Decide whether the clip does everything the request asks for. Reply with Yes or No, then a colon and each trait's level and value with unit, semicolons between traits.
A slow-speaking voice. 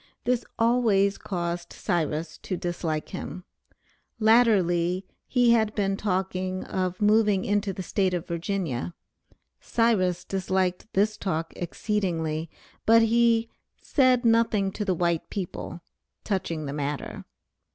Yes: slow, 120 wpm